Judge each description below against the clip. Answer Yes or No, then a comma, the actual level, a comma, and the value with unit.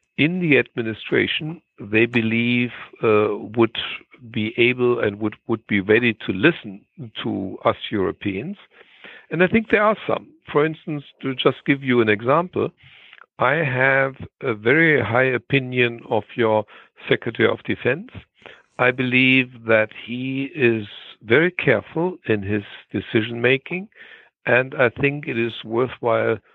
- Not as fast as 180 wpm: Yes, average, 140 wpm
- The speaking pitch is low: Yes, low, 120 Hz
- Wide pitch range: No, average, 3.6 semitones